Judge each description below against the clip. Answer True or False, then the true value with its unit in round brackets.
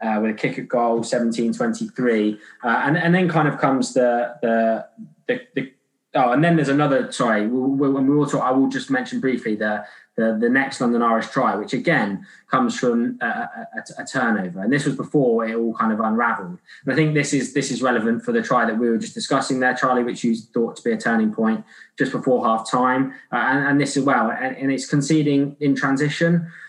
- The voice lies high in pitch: False (135 Hz)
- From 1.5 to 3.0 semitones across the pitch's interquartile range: False (4.0 semitones)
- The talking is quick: True (225 wpm)